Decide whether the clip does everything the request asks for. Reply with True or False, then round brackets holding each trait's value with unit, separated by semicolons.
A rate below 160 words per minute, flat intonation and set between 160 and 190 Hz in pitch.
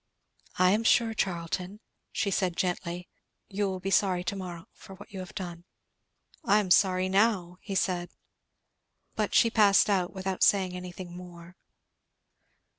True (150 wpm; 1.9 semitones; 185 Hz)